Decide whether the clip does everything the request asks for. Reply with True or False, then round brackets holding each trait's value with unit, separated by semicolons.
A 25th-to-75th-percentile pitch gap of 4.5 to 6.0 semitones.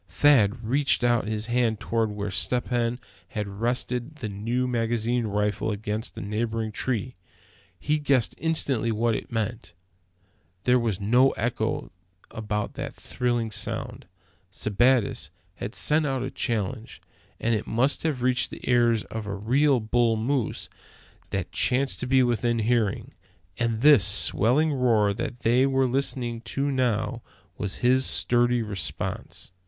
False (2.8 semitones)